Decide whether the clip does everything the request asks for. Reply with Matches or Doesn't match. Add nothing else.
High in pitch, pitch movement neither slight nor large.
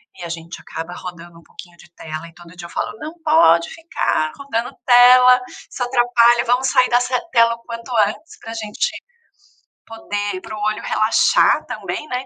Doesn't match